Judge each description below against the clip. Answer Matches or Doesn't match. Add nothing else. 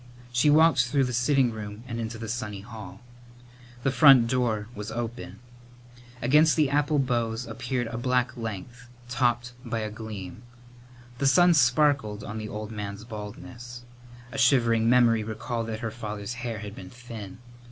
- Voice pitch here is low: Matches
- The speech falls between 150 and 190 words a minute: Matches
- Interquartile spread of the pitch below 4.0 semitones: Matches